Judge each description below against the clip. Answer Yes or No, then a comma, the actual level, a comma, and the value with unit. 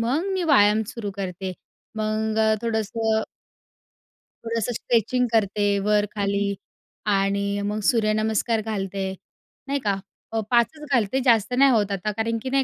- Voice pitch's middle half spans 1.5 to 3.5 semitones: Yes, narrow, 2.4 semitones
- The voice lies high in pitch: Yes, high, 220 Hz